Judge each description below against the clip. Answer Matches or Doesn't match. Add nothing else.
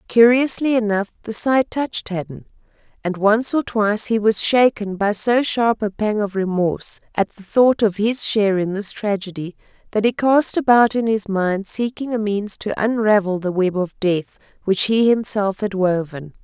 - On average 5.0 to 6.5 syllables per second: Doesn't match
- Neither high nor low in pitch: Doesn't match